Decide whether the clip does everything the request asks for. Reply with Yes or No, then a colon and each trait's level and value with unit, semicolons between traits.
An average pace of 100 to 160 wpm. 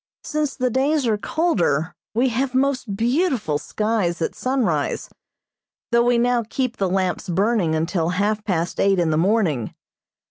Yes: average, 150 wpm